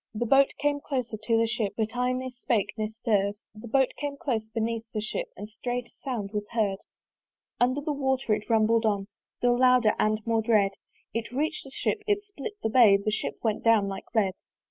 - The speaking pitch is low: No, high, 230 Hz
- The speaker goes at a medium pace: No, fast, 210 wpm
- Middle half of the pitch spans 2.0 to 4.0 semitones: Yes, average, 3.1 semitones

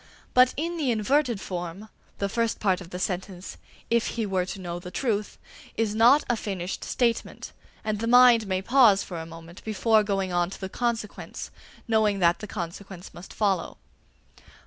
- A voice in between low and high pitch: No, high, 205 Hz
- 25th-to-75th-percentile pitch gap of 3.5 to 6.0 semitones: Yes, average, 4.0 semitones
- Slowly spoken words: No, average, 175 wpm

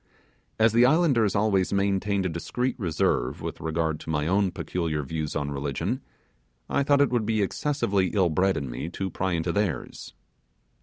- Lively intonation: No, average, 5.0 semitones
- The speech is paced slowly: No, average, 170 wpm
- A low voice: Yes, very low, 95 Hz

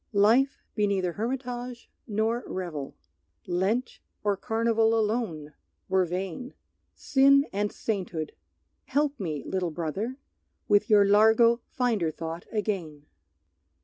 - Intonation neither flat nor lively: Yes, average, 4.7 semitones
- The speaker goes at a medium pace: No, slow, 110 wpm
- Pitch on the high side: Yes, high, 210 Hz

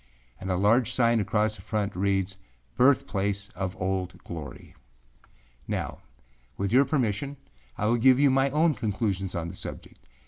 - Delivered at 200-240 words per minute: No, average, 150 wpm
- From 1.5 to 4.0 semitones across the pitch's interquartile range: No, average, 4.8 semitones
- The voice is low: Yes, low, 105 Hz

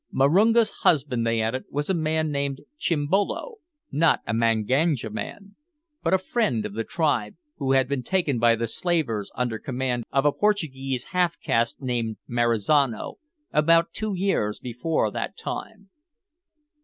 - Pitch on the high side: No, medium, 140 Hz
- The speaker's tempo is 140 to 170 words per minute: Yes, average, 145 wpm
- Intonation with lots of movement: Yes, wide, 6.2 semitones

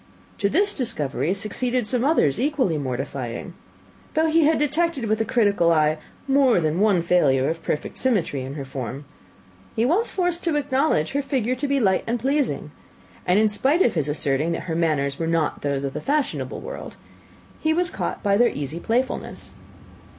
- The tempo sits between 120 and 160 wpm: No, average, 180 wpm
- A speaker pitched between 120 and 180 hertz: No, high, 210 Hz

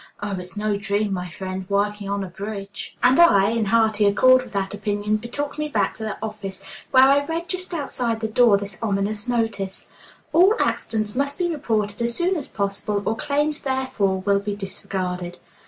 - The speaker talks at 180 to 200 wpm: Yes, average, 190 wpm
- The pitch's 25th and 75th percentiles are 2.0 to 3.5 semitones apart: No, average, 4.4 semitones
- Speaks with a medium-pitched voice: No, high, 215 Hz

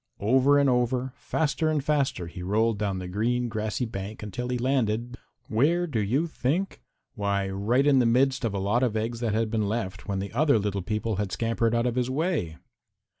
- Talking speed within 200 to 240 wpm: Yes, fast, 205 wpm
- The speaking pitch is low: Yes, low, 115 Hz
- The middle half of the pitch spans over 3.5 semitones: Yes, average, 4.0 semitones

